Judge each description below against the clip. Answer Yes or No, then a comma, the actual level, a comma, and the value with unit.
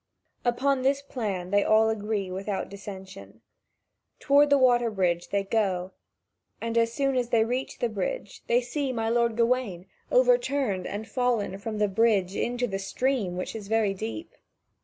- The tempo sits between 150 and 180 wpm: Yes, average, 160 wpm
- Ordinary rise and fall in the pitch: Yes, average, 4.1 semitones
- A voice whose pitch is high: Yes, high, 225 Hz